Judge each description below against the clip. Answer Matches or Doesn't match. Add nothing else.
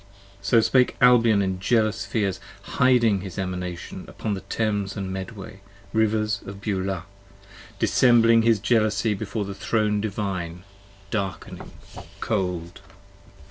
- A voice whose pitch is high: Doesn't match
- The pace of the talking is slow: Matches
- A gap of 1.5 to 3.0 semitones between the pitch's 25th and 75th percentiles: Matches